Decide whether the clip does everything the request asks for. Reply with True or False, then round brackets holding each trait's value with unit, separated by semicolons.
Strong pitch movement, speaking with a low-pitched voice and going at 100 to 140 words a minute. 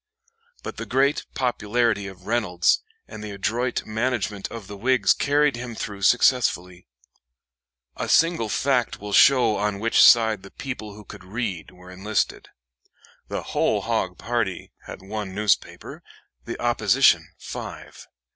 False (3.6 semitones; 110 Hz; 135 wpm)